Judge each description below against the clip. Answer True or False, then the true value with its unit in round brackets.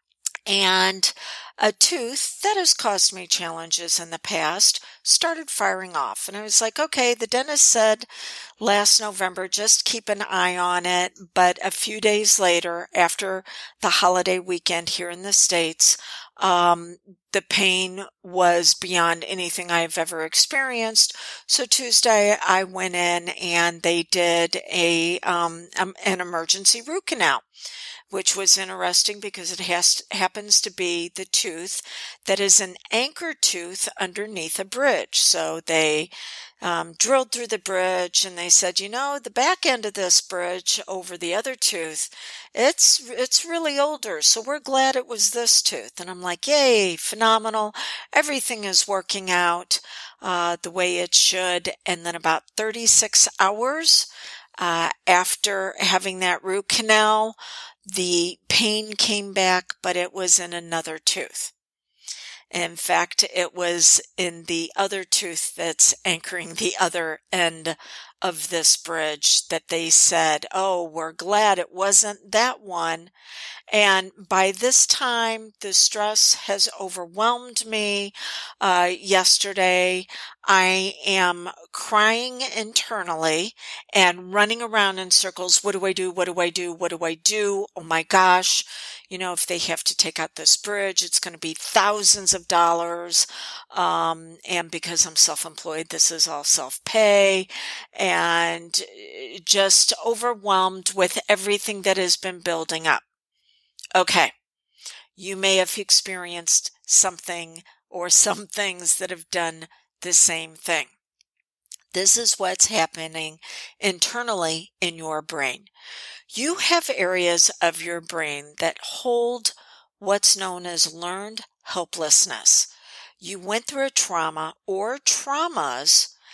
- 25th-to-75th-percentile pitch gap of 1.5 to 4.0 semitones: True (3.6 semitones)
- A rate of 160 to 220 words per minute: False (140 wpm)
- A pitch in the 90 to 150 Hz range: False (185 Hz)